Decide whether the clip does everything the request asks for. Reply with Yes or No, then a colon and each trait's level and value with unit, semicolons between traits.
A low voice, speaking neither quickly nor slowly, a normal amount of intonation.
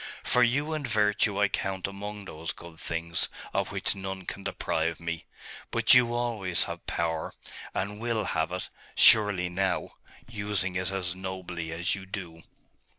Yes: very low, 95 Hz; average, 155 wpm; average, 3.3 semitones